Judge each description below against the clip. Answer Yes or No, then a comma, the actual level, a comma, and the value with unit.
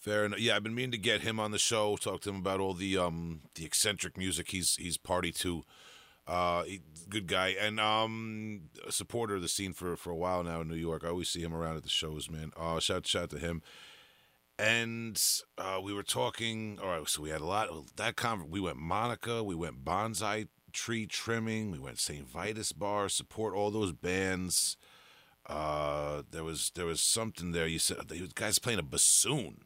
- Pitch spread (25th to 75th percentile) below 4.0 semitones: No, average, 4.5 semitones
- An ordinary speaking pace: No, fast, 215 wpm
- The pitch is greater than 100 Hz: No, very low, 95 Hz